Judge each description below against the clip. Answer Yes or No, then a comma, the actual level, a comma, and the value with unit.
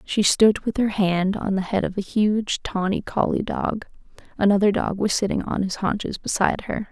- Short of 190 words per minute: No, average, 200 wpm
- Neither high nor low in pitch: No, high, 200 Hz